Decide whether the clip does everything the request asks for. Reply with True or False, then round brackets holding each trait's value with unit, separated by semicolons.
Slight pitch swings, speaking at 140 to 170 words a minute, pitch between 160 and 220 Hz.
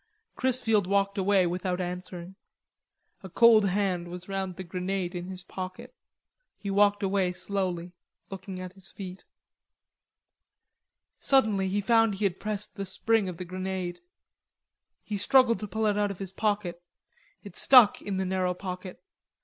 True (2.1 semitones; 150 wpm; 190 Hz)